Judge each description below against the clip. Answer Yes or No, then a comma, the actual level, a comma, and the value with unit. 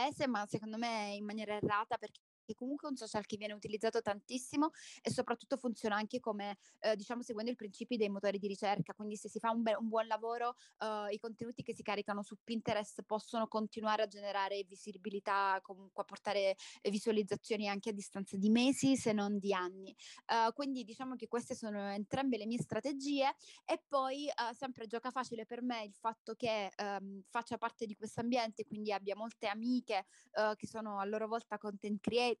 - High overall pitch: Yes, high, 220 Hz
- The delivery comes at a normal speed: No, fast, 190 wpm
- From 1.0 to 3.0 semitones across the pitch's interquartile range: Yes, narrow, 2.4 semitones